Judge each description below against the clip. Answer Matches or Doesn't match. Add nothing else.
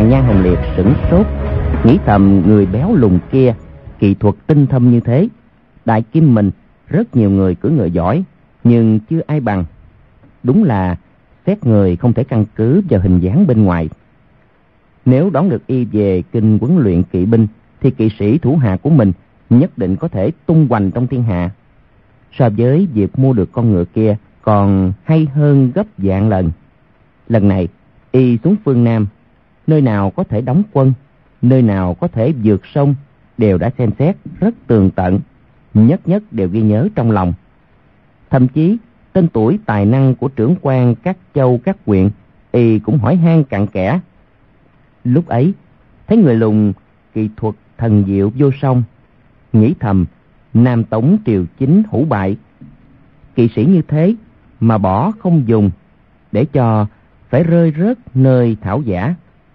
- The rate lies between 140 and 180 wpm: Matches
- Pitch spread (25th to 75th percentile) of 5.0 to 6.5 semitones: Matches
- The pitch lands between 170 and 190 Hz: Doesn't match